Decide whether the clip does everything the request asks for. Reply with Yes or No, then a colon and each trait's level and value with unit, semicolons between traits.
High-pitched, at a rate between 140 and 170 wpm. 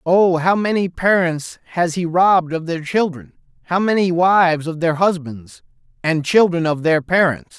No: medium, 170 Hz; average, 165 wpm